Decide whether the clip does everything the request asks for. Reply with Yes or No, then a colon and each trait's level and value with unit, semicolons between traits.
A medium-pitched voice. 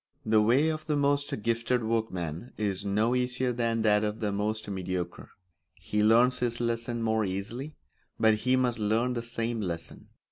No: low, 115 Hz